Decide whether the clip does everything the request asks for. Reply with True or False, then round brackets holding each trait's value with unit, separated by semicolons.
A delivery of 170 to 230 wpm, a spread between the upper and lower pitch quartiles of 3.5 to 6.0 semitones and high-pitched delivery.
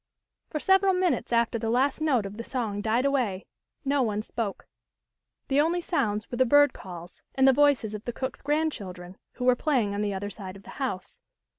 True (200 wpm; 5.6 semitones; 240 Hz)